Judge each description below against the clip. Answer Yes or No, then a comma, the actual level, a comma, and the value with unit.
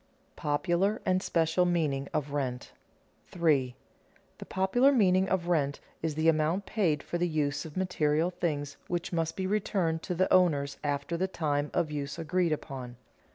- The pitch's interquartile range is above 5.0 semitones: No, average, 3.8 semitones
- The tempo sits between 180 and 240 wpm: No, average, 165 wpm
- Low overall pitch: No, medium, 165 Hz